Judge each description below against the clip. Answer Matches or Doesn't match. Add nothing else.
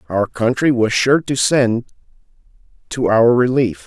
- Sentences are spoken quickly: Doesn't match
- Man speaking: Matches